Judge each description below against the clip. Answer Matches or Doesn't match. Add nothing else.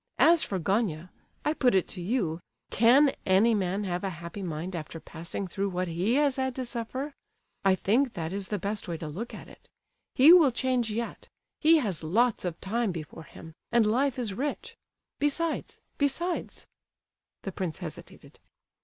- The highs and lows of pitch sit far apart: Matches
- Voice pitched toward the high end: Matches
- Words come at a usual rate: Matches